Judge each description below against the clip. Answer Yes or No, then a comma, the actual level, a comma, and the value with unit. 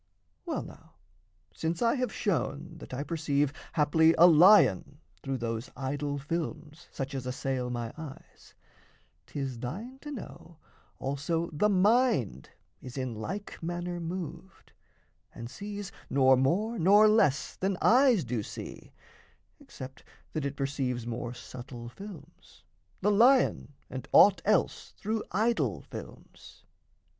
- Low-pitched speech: No, medium, 155 Hz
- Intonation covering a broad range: Yes, wide, 6.9 semitones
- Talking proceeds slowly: Yes, slow, 130 wpm